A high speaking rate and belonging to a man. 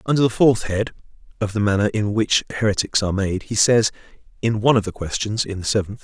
Yes: fast, 220 wpm; male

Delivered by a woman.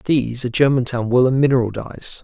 No: male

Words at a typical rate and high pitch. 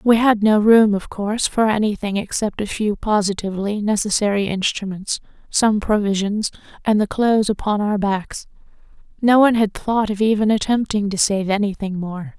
Yes: average, 170 wpm; high, 210 Hz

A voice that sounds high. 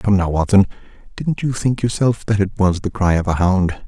No: low, 100 Hz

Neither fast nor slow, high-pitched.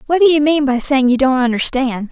No: fast, 255 wpm; very high, 270 Hz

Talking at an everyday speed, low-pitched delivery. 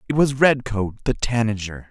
Yes: average, 160 wpm; low, 115 Hz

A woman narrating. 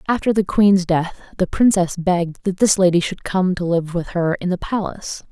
Yes: female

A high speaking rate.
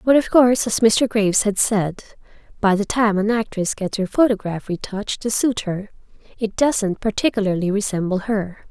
No: average, 170 wpm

